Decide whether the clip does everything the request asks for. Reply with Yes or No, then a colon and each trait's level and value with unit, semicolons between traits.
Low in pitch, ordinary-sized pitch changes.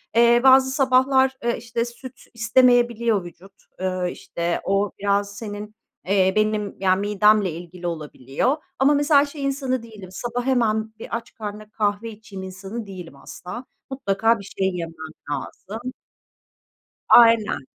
No: high, 215 Hz; average, 4.0 semitones